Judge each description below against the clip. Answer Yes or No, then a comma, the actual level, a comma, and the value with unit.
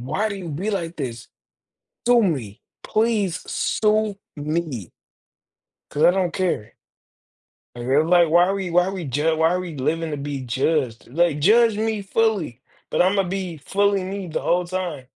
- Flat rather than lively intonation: No, average, 4.9 semitones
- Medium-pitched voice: Yes, medium, 175 Hz